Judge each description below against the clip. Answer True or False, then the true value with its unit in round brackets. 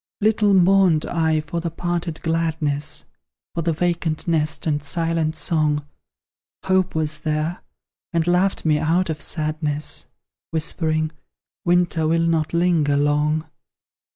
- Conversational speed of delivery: False (125 wpm)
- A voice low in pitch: False (160 Hz)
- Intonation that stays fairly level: True (2.0 semitones)